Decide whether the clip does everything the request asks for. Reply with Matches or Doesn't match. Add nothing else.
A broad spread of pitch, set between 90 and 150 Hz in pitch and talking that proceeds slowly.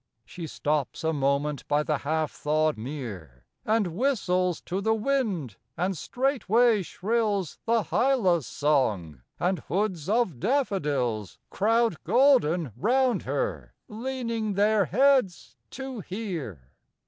Doesn't match